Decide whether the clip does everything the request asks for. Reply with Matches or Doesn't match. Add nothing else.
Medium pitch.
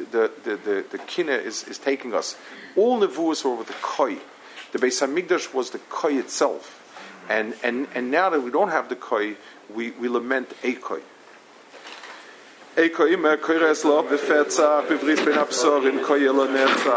Matches